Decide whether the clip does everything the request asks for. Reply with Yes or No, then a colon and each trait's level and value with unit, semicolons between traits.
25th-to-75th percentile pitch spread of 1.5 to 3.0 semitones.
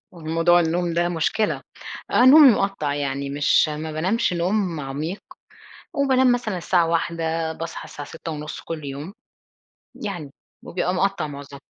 No: average, 3.8 semitones